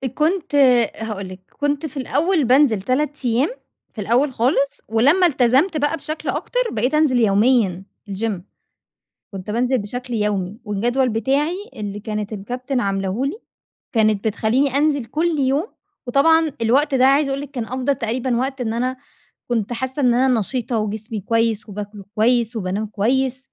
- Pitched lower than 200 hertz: No, high, 245 Hz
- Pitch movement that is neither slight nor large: Yes, average, 4.2 semitones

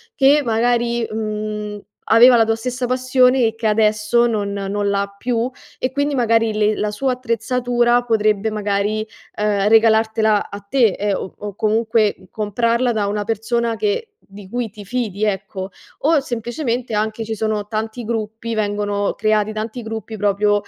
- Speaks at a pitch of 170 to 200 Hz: No, high, 220 Hz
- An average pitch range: No, narrow, 2.3 semitones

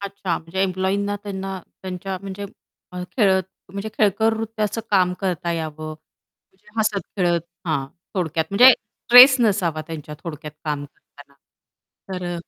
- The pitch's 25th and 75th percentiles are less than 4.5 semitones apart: Yes, average, 3.5 semitones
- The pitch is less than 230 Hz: Yes, high, 190 Hz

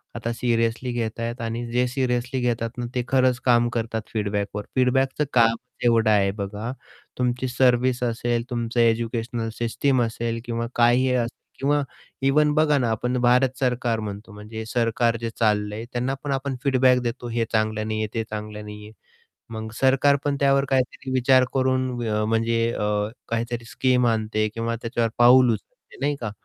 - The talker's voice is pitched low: Yes, low, 120 Hz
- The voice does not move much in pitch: Yes, narrow, 2.1 semitones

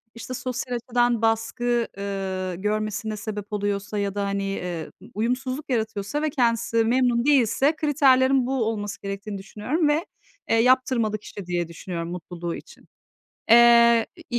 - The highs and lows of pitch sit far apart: No, average, 3.9 semitones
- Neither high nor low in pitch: No, high, 225 Hz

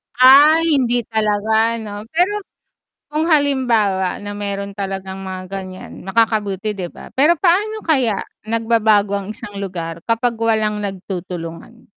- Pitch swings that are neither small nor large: Yes, average, 4.3 semitones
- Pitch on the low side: No, high, 215 Hz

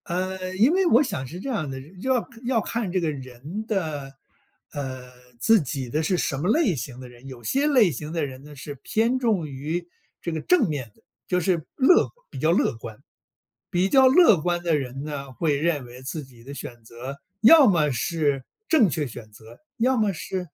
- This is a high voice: No, medium, 160 Hz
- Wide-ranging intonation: Yes, wide, 7.5 semitones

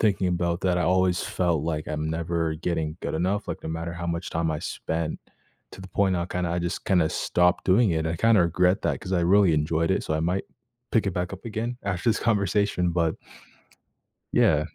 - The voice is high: No, very low, 90 Hz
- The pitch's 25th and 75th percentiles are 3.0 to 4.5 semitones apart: No, narrow, 2.5 semitones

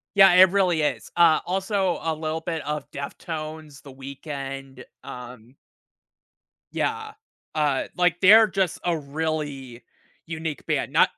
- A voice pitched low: No, medium, 155 Hz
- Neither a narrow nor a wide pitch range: Yes, average, 4.2 semitones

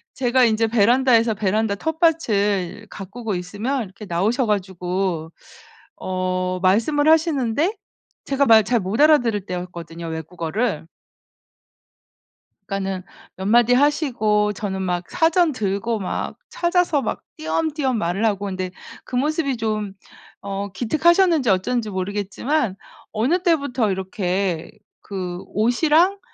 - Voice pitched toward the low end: No, high, 215 Hz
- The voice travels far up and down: Yes, wide, 6.0 semitones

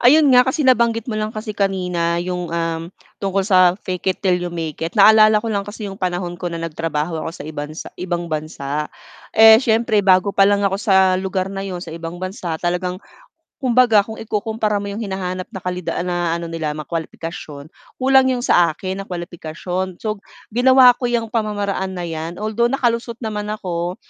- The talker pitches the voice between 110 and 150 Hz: No, high, 190 Hz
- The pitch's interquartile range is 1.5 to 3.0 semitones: No, average, 3.9 semitones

